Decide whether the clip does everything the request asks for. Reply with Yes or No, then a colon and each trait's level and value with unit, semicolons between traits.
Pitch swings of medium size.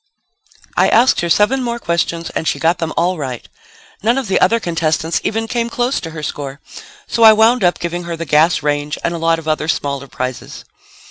No: wide, 6.2 semitones